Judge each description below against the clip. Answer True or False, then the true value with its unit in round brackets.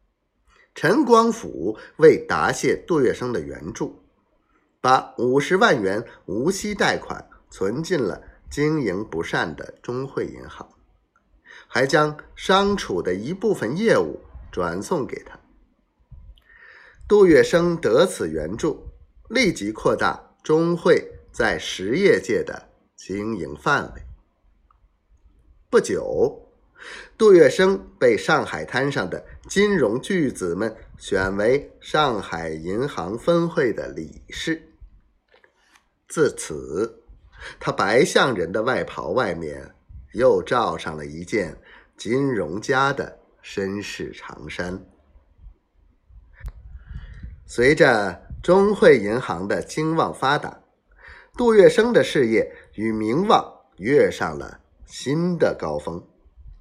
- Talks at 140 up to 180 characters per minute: True (155 characters per minute)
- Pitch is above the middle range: False (170 Hz)